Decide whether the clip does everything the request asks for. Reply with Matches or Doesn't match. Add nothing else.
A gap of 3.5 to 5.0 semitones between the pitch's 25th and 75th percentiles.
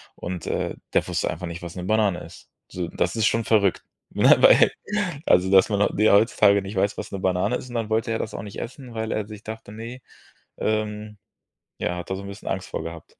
Doesn't match